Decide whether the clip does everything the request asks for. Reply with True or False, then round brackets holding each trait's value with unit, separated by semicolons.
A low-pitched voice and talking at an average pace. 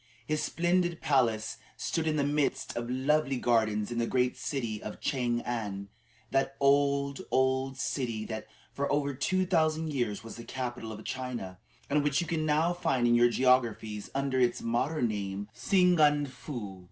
True (130 Hz; 170 wpm)